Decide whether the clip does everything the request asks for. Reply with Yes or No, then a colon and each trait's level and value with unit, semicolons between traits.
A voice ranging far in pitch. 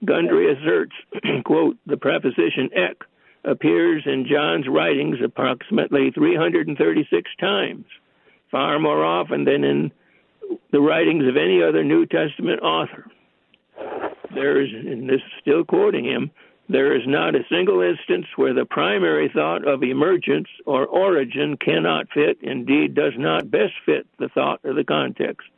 No: average, 3.8 semitones